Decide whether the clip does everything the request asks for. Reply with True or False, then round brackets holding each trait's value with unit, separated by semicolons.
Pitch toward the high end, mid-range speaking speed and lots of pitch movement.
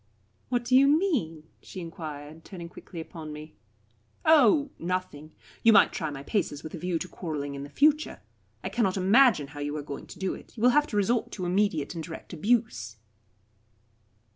False (175 Hz; 190 wpm; 7.3 semitones)